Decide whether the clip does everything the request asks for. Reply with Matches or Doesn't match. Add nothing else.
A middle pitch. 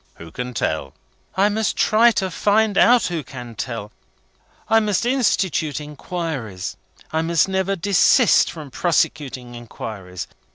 Matches